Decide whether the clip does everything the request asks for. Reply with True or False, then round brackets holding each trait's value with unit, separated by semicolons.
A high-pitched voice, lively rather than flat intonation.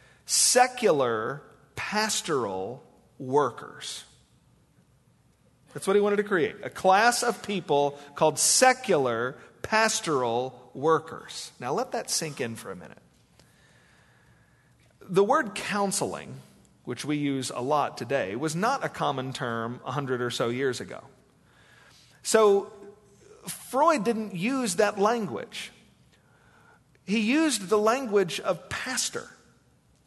True (195 Hz; 7.7 semitones)